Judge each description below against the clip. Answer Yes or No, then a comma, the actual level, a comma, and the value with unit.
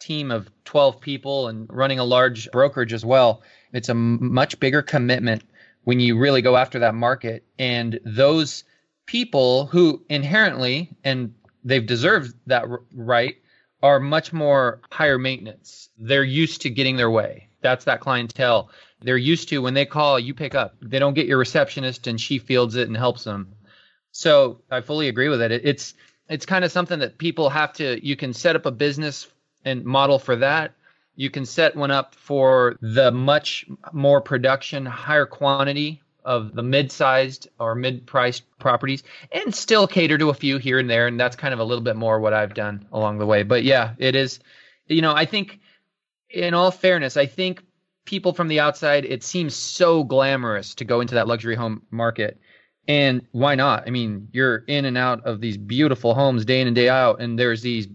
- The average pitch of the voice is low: Yes, low, 130 Hz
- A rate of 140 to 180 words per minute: No, average, 190 wpm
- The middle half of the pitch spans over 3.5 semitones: No, average, 3.2 semitones